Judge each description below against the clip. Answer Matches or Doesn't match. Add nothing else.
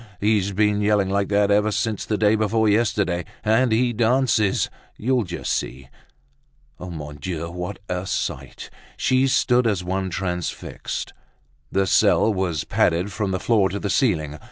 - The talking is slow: Doesn't match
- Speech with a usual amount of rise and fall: Matches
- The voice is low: Matches